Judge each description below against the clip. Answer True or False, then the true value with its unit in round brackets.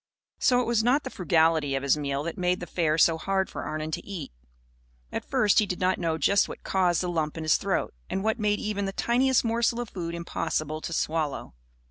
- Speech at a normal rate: False (225 wpm)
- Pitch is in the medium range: True (180 Hz)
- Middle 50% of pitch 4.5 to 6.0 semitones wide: True (4.9 semitones)